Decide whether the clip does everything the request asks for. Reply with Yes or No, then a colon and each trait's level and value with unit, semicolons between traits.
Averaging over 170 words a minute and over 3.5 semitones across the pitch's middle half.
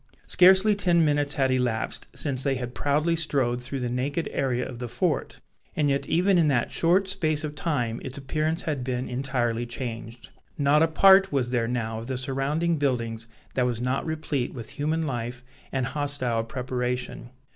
Yes: average, 180 wpm; average, 4.0 semitones